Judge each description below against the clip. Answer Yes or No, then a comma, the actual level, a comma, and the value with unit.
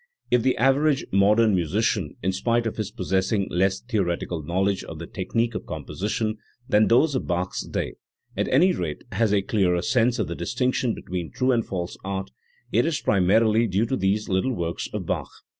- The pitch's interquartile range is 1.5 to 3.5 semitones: No, average, 4.0 semitones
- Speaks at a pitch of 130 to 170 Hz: No, low, 105 Hz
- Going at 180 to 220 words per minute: Yes, average, 185 wpm